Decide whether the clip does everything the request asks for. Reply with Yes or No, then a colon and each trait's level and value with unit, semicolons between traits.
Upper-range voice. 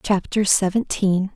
Yes: high, 195 Hz